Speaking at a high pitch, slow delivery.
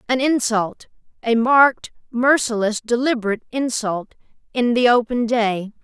Yes: high, 235 Hz; slow, 105 wpm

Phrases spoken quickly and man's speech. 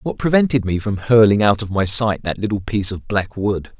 Yes: fast, 235 wpm; male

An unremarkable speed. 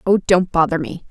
No: fast, 215 wpm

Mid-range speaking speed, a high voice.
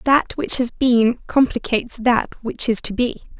Yes: average, 175 wpm; high, 245 Hz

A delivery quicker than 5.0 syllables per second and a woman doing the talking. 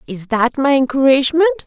Yes: 5.3 syllables/s; female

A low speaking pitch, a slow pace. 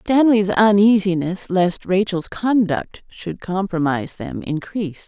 No: high, 190 Hz; slow, 105 wpm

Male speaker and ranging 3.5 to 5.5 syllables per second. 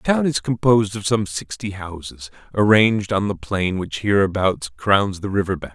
Yes: male; 5.0 syllables/s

